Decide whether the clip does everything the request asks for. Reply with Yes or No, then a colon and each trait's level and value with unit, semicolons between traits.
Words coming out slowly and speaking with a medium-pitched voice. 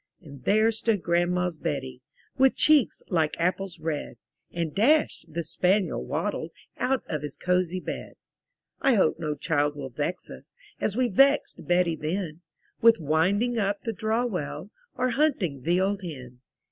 No: average, 155 wpm; medium, 180 Hz